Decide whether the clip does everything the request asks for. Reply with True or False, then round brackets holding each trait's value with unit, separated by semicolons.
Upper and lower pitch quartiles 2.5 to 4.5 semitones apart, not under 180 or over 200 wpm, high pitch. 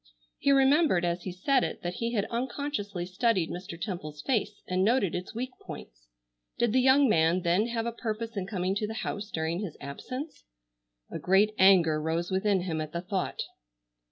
False (5.0 semitones; 185 wpm; 195 Hz)